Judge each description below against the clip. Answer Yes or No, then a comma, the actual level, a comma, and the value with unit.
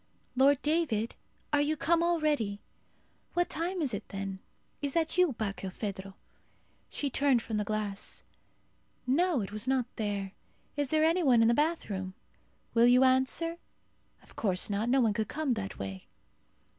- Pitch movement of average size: No, wide, 6.9 semitones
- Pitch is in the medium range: No, very high, 250 Hz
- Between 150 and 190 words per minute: Yes, average, 155 wpm